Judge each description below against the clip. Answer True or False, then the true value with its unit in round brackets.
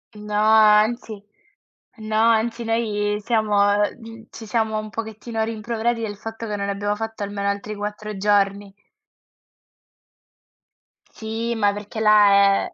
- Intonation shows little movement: True (1.5 semitones)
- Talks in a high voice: True (215 Hz)